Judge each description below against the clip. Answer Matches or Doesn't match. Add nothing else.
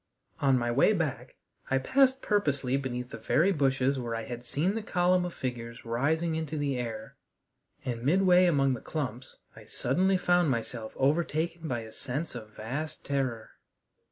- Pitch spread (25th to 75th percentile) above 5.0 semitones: Matches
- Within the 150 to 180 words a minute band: Matches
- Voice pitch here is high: Doesn't match